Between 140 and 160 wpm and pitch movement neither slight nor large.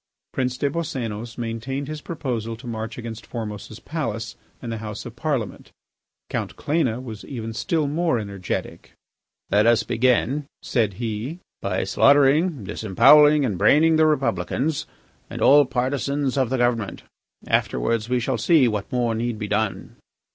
Yes: average, 145 wpm; average, 4.2 semitones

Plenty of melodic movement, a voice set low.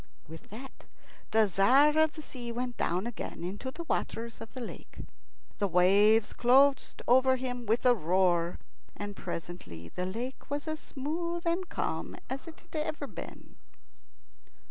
No: wide, 6.3 semitones; high, 245 Hz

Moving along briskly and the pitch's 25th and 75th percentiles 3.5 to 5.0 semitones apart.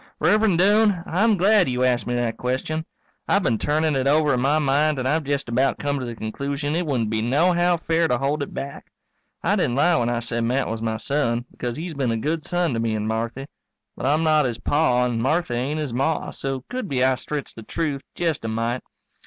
Yes: fast, 235 wpm; average, 4.7 semitones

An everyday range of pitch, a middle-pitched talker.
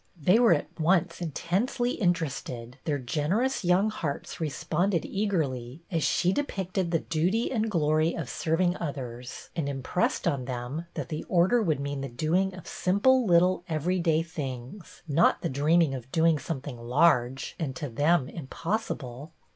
Yes: average, 4.6 semitones; medium, 165 Hz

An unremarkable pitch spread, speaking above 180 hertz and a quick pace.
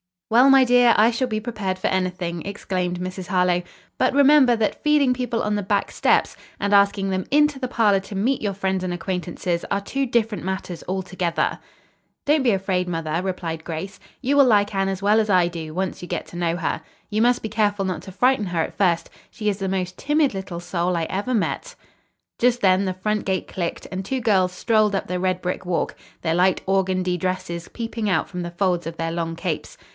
Yes: average, 3.4 semitones; high, 190 Hz; fast, 215 wpm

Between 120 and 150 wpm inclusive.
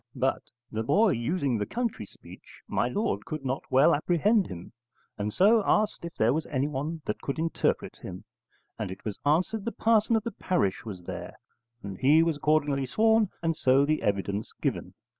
No: average, 180 wpm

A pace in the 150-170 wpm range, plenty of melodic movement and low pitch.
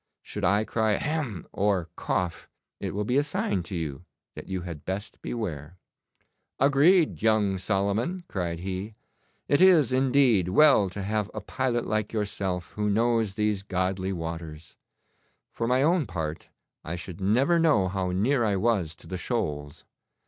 No: average, 155 wpm; average, 4.8 semitones; low, 100 Hz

